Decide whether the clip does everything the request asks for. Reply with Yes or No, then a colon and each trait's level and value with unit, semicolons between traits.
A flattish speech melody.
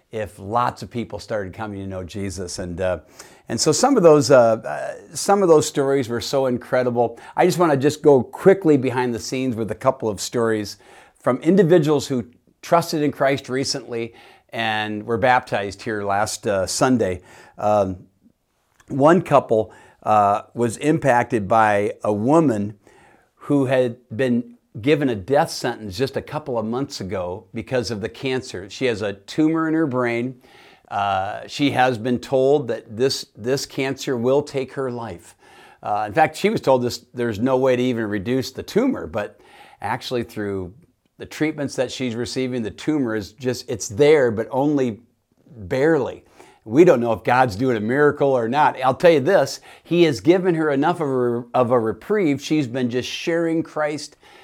No: average, 3.9 semitones